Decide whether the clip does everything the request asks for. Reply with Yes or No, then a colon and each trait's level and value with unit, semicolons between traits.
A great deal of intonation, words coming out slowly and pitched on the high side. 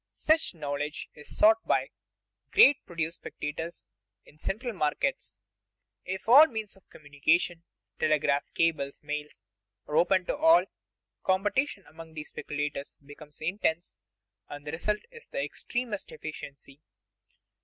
No: wide, 6.0 semitones; slow, 130 wpm; medium, 165 Hz